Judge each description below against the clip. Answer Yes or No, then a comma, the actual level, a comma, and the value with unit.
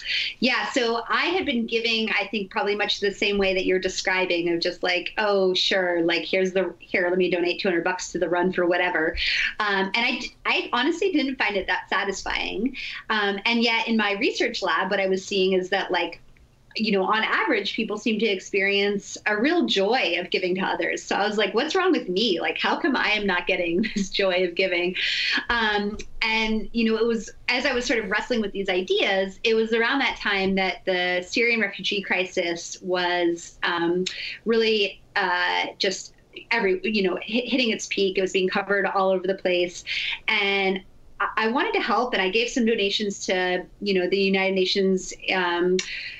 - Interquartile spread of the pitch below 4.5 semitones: Yes, average, 3.3 semitones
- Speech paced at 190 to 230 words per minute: Yes, fast, 205 wpm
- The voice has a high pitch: Yes, high, 195 Hz